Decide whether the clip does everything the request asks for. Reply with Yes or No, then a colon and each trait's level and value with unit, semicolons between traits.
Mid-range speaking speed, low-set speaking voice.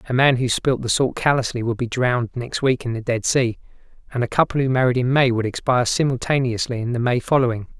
No: fast, 230 wpm; low, 125 Hz